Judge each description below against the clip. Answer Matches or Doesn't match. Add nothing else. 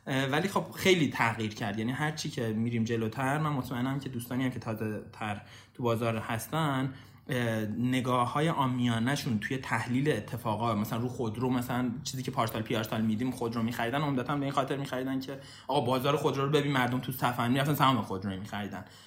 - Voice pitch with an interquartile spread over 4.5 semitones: Doesn't match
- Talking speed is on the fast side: Matches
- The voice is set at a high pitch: Doesn't match